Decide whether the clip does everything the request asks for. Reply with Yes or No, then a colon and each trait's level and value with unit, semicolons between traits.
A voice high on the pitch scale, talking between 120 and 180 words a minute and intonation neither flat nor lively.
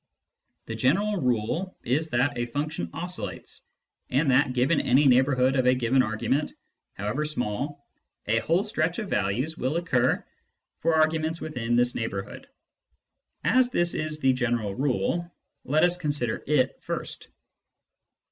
No: low, 135 Hz; average, 140 wpm; average, 4.5 semitones